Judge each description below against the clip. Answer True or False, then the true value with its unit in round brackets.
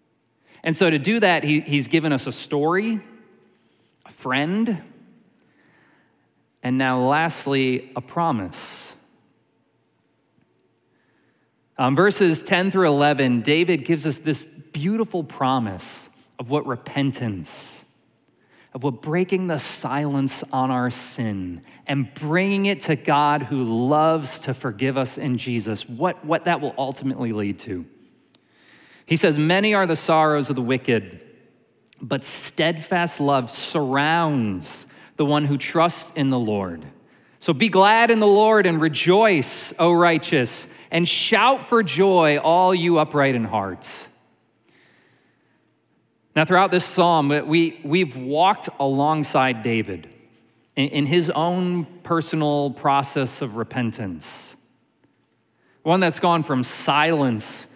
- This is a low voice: False (150 Hz)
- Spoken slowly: True (125 wpm)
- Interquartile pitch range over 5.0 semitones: False (4.5 semitones)